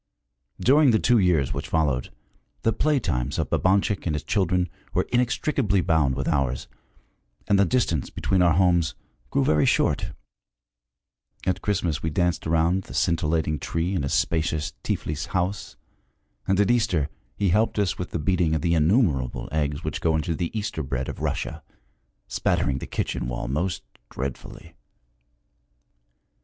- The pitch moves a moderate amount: Yes, average, 4.7 semitones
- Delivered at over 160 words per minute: No, average, 155 wpm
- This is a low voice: Yes, very low, 85 Hz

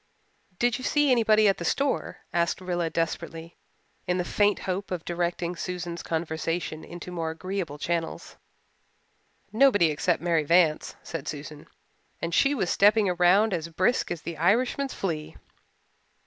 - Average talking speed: Yes, average, 145 wpm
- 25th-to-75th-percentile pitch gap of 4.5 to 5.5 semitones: No, average, 3.6 semitones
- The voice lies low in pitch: No, medium, 175 Hz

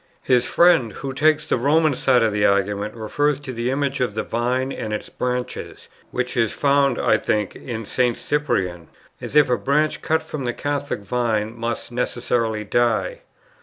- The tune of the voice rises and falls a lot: No, average, 4.2 semitones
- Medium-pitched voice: No, low, 125 Hz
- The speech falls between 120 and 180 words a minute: Yes, average, 175 wpm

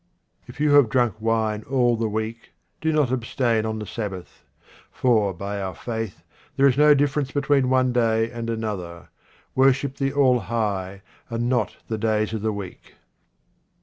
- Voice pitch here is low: Yes, low, 115 Hz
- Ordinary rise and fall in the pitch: Yes, average, 3.4 semitones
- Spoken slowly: No, average, 165 wpm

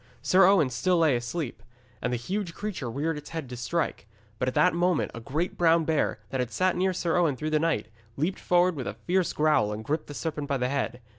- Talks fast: Yes, fast, 235 wpm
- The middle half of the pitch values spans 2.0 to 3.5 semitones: No, wide, 5.6 semitones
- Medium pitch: Yes, medium, 155 Hz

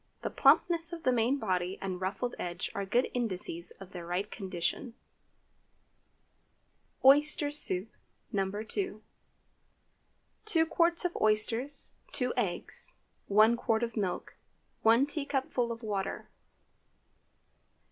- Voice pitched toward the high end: Yes, high, 225 Hz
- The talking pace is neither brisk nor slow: No, slow, 115 wpm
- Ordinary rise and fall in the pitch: No, wide, 6.4 semitones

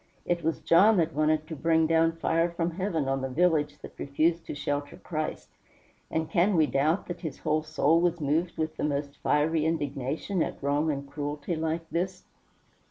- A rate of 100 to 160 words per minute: No, average, 185 wpm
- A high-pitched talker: No, medium, 160 Hz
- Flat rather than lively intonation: Yes, narrow, 2.3 semitones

